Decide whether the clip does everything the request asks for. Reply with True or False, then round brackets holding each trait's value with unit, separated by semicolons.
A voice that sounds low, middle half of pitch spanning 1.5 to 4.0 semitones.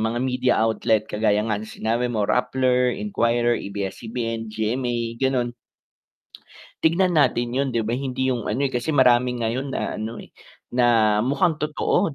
True (120 Hz; 2.6 semitones)